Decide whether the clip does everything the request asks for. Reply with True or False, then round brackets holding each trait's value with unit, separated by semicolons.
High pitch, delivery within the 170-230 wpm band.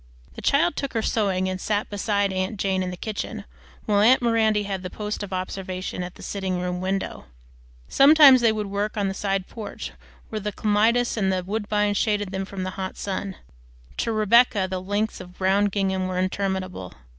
True (200 Hz; 190 wpm)